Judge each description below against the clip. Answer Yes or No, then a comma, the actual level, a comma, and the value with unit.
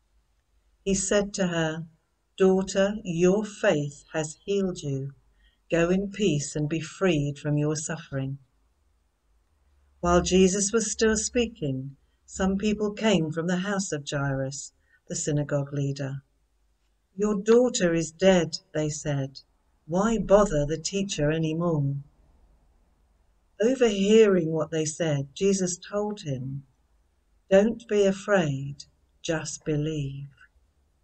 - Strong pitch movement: Yes, wide, 6.0 semitones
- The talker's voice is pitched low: No, medium, 155 Hz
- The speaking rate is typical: No, slow, 115 wpm